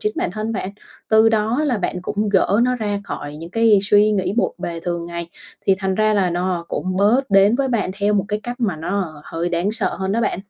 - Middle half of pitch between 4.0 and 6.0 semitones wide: No, average, 3.4 semitones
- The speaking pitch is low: No, high, 200 Hz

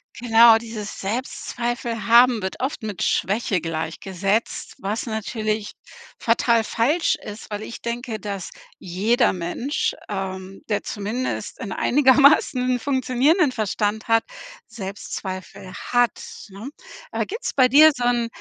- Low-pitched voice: No, high, 225 Hz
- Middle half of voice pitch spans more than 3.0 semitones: Yes, average, 3.5 semitones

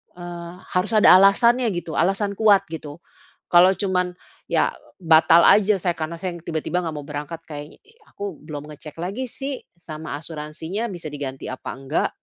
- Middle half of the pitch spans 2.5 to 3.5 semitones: No, average, 4.1 semitones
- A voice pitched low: No, medium, 170 Hz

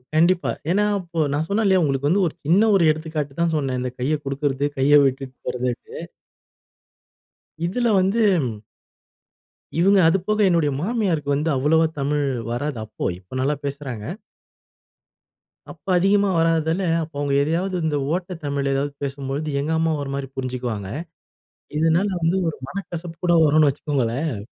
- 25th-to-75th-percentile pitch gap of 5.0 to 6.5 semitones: No, average, 4.0 semitones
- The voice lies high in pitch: No, medium, 150 Hz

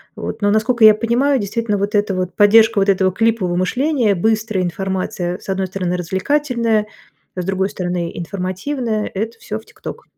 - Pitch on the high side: Yes, high, 205 Hz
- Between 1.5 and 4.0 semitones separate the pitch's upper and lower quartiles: Yes, average, 3.4 semitones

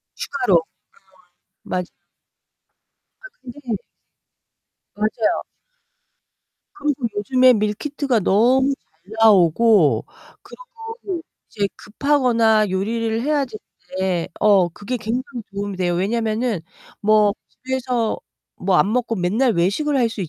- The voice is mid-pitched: No, high, 225 Hz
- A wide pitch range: No, average, 4.5 semitones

